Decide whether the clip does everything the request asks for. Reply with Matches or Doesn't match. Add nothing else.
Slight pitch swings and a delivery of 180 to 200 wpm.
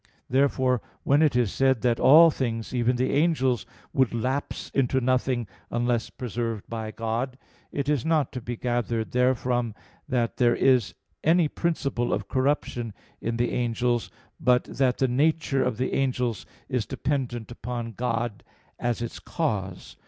Doesn't match